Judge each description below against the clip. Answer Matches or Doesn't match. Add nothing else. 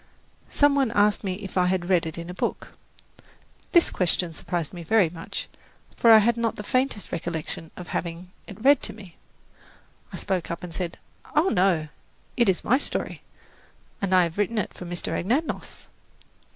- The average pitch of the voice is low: Doesn't match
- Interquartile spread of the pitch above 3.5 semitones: Matches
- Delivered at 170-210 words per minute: Matches